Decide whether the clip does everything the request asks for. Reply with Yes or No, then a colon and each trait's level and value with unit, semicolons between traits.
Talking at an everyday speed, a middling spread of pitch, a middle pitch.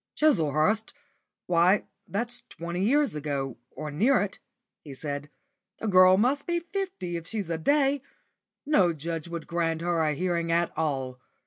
No: average, 150 wpm; wide, 5.9 semitones; medium, 170 Hz